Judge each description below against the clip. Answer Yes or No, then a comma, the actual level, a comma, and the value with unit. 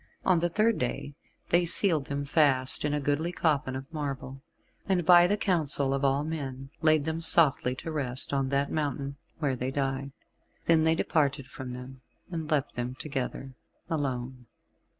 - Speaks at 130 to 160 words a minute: No, average, 170 wpm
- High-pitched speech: No, medium, 140 Hz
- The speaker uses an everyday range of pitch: Yes, average, 3.2 semitones